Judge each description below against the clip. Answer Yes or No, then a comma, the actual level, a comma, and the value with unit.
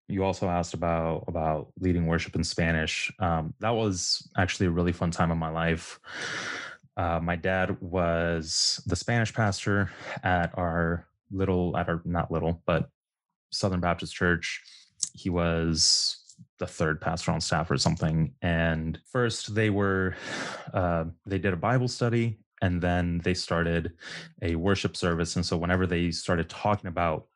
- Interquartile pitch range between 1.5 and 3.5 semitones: Yes, average, 2.8 semitones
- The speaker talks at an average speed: Yes, average, 155 wpm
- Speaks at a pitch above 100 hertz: No, very low, 90 Hz